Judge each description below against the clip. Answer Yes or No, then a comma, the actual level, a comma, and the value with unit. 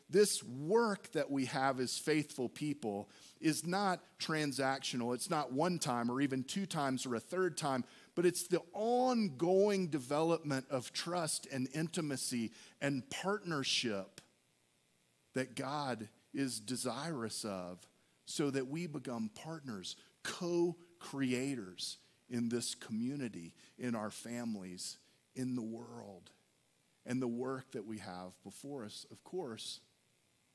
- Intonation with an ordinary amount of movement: No, wide, 5.9 semitones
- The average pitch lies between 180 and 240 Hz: No, low, 135 Hz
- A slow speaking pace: Yes, slow, 130 wpm